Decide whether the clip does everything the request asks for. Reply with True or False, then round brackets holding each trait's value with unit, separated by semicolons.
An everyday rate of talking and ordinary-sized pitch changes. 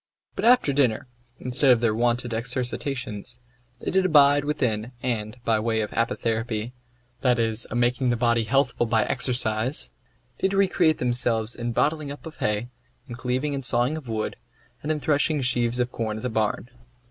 True (170 wpm; 3.4 semitones)